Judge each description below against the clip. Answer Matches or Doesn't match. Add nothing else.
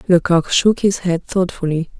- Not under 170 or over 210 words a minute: Doesn't match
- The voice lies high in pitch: Doesn't match